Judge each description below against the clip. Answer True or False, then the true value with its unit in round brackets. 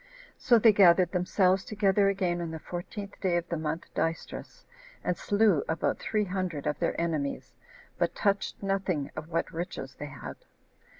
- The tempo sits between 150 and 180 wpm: True (165 wpm)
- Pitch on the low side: False (180 Hz)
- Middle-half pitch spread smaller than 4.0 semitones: True (3.0 semitones)